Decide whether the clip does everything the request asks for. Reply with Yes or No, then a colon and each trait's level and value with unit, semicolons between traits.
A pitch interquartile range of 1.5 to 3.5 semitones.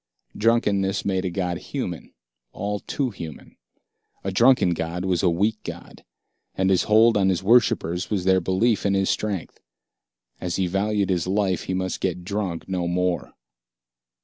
Yes: narrow, 2.6 semitones